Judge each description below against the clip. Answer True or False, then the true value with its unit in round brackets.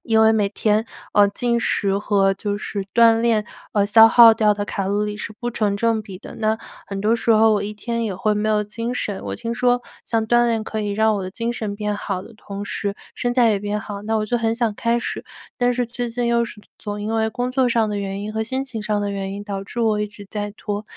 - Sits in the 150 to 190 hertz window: False (215 Hz)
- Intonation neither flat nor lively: False (2.1 semitones)